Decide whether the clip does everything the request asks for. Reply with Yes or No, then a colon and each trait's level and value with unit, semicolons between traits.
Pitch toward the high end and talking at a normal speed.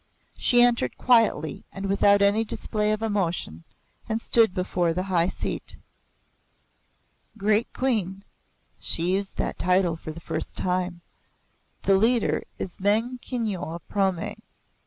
No: high, 195 Hz; slow, 130 wpm